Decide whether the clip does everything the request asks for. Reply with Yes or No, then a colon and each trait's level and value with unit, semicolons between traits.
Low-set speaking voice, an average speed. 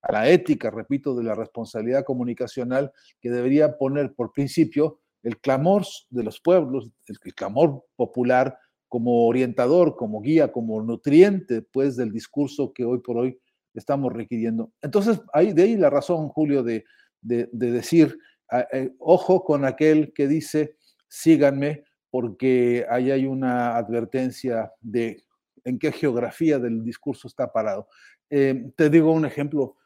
Yes: low, 130 Hz; average, 145 wpm